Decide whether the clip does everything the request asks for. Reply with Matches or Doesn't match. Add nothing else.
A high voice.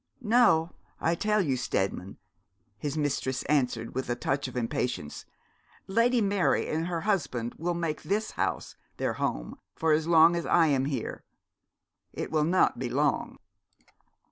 Doesn't match